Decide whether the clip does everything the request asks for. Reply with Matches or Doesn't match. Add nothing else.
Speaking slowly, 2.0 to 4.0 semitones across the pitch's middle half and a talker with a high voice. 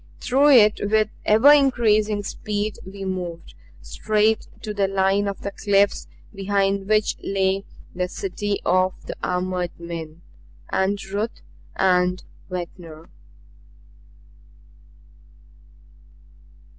Matches